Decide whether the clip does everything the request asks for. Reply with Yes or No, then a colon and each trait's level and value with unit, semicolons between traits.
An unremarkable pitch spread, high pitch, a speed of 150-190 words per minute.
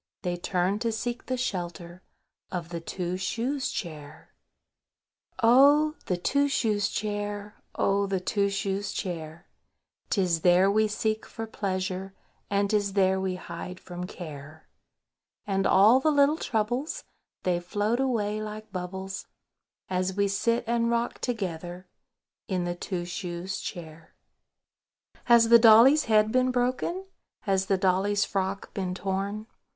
No: average, 3.7 semitones; high, 200 Hz; slow, 135 wpm